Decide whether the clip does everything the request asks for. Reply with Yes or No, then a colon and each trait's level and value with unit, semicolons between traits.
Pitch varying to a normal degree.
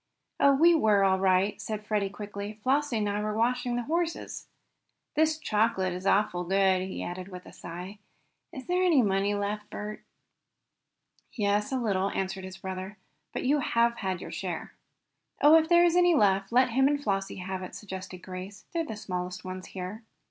Yes: average, 5.0 semitones